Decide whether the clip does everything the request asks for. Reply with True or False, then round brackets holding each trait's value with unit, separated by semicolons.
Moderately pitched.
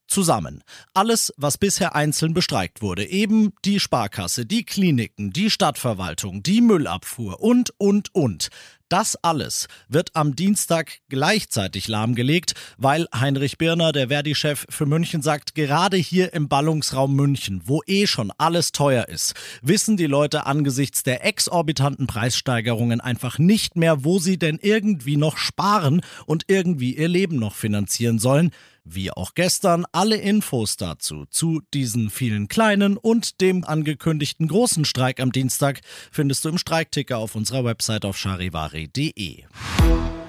True (150 Hz)